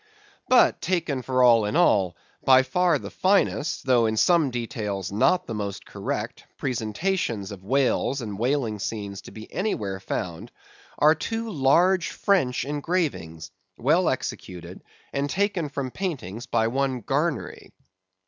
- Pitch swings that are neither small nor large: No, wide, 7.5 semitones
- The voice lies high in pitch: No, low, 130 Hz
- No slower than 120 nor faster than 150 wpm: Yes, average, 140 wpm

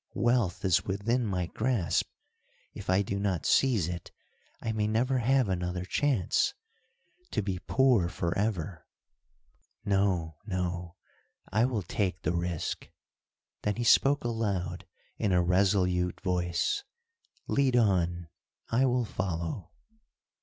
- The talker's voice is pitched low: Yes, very low, 95 Hz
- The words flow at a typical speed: No, slow, 120 wpm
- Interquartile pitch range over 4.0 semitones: Yes, average, 4.4 semitones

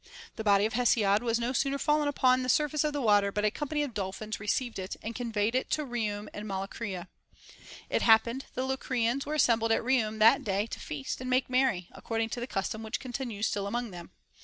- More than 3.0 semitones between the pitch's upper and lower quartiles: Yes, average, 3.7 semitones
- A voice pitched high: Yes, high, 230 Hz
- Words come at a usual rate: No, fast, 215 wpm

